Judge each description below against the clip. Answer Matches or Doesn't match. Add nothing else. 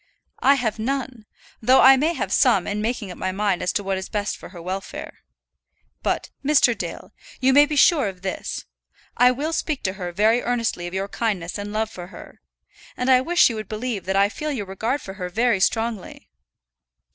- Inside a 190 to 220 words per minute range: Matches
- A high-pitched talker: Matches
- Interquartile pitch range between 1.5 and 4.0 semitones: Doesn't match